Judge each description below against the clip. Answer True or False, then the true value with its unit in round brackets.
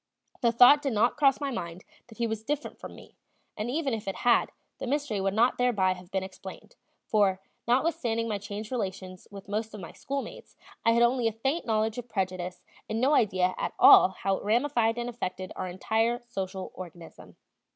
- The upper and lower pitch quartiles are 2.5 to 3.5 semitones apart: False (4.2 semitones)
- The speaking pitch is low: False (220 Hz)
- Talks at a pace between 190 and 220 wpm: True (195 wpm)